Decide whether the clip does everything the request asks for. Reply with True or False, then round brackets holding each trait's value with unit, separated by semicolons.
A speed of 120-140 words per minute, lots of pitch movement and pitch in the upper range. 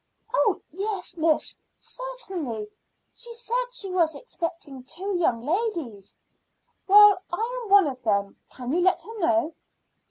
True (135 wpm; 6.7 semitones; 355 Hz)